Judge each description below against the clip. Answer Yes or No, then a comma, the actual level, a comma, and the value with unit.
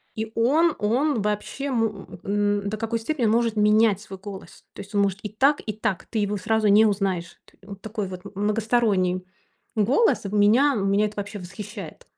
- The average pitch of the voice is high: Yes, high, 210 Hz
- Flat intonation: Yes, narrow, 2.2 semitones